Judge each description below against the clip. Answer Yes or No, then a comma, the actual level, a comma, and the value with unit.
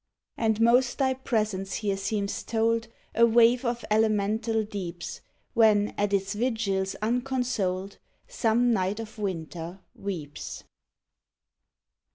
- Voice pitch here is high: Yes, high, 215 Hz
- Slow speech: Yes, slow, 110 wpm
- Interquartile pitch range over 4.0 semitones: No, average, 3.1 semitones